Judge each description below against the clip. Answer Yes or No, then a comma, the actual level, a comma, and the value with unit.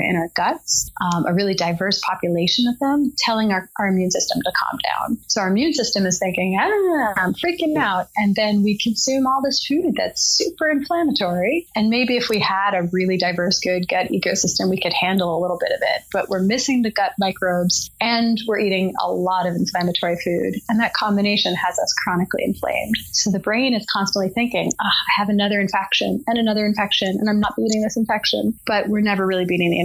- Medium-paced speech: No, fast, 210 wpm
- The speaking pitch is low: No, high, 205 Hz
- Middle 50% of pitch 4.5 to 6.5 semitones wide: No, average, 3.9 semitones